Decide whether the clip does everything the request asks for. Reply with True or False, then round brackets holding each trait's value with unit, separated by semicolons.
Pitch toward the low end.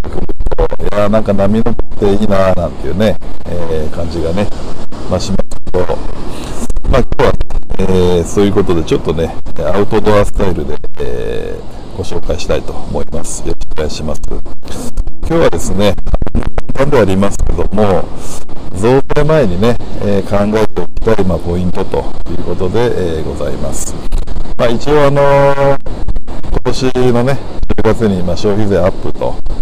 True (100 Hz)